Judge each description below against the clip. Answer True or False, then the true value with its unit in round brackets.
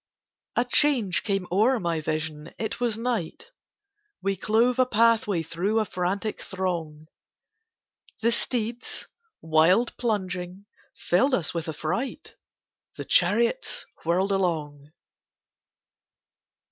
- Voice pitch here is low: False (195 Hz)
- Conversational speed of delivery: False (100 wpm)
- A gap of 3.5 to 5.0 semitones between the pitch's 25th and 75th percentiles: False (5.4 semitones)